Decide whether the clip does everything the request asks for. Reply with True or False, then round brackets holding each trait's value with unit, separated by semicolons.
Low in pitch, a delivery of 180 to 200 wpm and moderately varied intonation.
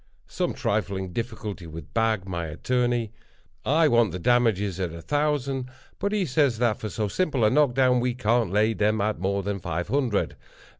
True (110 Hz; 185 wpm; 4.6 semitones)